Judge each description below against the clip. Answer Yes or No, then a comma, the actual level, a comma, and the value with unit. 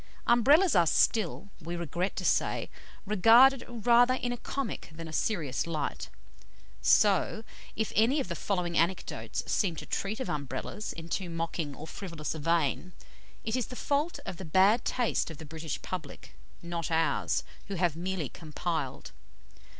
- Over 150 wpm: Yes, average, 160 wpm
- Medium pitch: Yes, medium, 180 Hz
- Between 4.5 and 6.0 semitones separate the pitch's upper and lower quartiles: Yes, wide, 5.4 semitones